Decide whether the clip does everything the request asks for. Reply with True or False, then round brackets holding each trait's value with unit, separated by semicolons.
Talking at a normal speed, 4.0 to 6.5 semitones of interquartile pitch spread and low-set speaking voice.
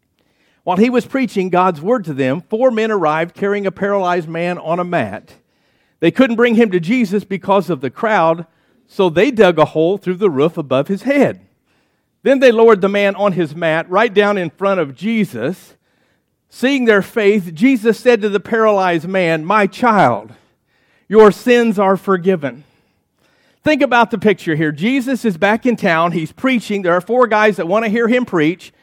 False (185 wpm; 4.6 semitones; 200 Hz)